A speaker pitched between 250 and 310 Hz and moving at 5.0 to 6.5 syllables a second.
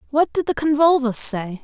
Yes: very high, 280 Hz; 5.8 syllables/s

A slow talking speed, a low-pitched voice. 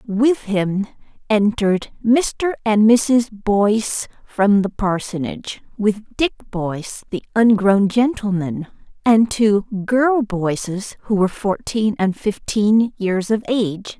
No: slow, 120 wpm; high, 210 Hz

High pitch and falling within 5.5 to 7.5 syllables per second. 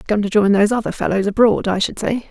Yes: high, 210 Hz; 6.7 syllables/s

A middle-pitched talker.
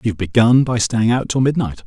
No: low, 115 Hz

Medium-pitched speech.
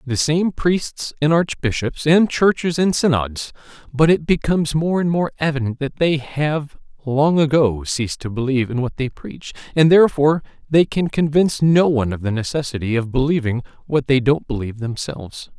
Yes: medium, 145 Hz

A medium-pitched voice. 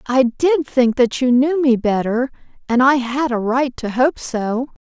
No: very high, 255 Hz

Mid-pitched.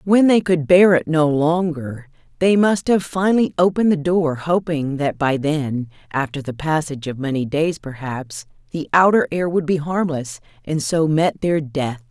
Yes: medium, 155 Hz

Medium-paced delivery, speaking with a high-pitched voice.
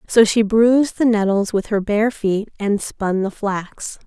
Yes: average, 190 wpm; high, 210 Hz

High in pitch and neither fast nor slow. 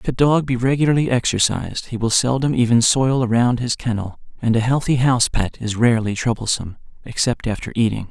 No: low, 120 Hz; average, 185 wpm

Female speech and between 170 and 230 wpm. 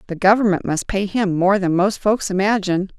Yes: female; average, 200 wpm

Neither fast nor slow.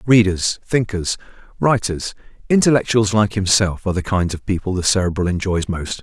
No: slow, 130 wpm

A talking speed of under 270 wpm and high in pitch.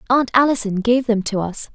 Yes: fast, 205 wpm; high, 230 Hz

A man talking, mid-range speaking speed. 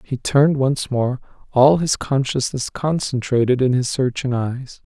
Yes: male; average, 145 wpm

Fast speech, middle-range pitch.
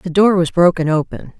Yes: fast, 215 wpm; medium, 175 Hz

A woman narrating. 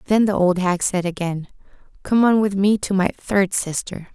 Yes: female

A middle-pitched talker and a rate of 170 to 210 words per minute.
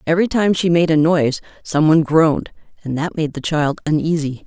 Yes: medium, 160 Hz; average, 200 wpm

